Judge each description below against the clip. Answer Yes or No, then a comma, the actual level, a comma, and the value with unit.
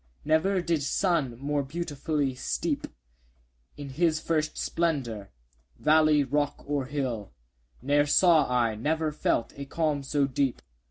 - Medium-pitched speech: Yes, medium, 145 Hz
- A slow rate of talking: Yes, slow, 130 wpm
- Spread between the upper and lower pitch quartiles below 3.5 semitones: Yes, average, 2.7 semitones